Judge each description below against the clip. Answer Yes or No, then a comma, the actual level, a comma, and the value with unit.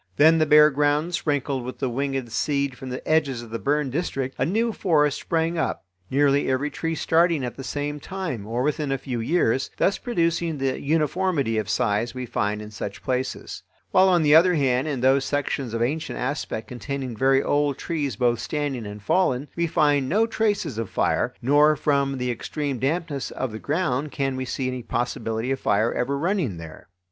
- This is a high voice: No, medium, 140 Hz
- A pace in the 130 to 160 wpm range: No, average, 195 wpm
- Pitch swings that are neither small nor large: Yes, average, 3.6 semitones